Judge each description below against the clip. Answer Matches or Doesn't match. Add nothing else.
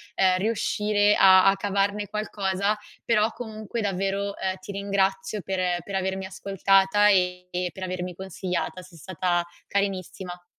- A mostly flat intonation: Matches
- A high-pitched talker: Matches